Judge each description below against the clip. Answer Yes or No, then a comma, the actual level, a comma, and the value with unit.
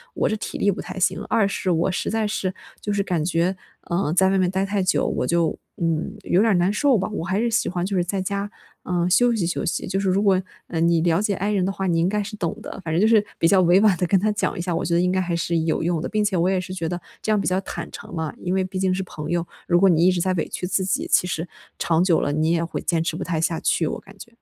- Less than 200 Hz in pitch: Yes, medium, 185 Hz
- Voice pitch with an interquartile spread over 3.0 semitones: No, narrow, 2.5 semitones